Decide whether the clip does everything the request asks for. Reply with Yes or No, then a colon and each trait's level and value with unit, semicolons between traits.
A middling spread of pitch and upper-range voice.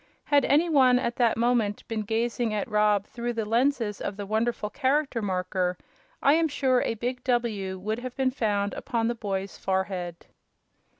Yes: average, 3.5 semitones; high, 230 Hz